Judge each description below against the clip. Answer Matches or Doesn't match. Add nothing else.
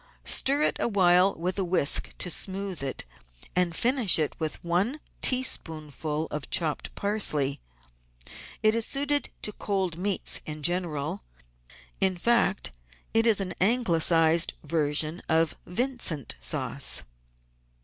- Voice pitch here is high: Doesn't match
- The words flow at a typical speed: Doesn't match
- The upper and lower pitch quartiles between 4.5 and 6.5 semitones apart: Matches